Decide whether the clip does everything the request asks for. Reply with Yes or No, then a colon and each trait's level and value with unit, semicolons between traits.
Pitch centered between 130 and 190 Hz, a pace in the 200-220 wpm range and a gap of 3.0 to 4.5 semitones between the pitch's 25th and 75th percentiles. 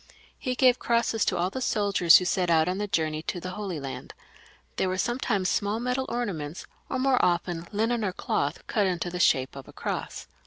No: medium, 185 Hz; fast, 205 wpm; average, 5.3 semitones